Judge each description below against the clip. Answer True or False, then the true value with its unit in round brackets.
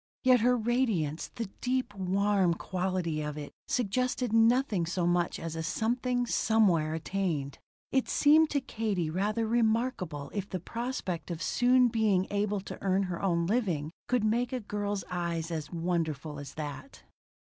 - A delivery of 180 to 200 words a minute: False (155 wpm)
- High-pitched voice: True (195 Hz)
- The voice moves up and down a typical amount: False (5.7 semitones)